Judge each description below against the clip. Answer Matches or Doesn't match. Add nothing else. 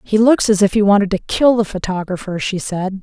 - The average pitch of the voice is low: Doesn't match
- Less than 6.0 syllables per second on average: Matches